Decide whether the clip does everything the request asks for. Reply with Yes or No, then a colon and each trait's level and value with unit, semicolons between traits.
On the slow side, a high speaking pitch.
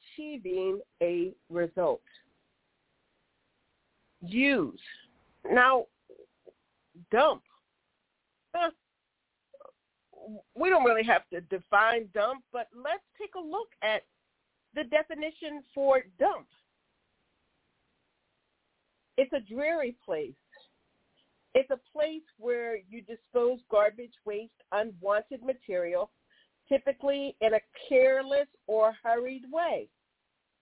Yes: slow, 90 wpm; very high, 265 Hz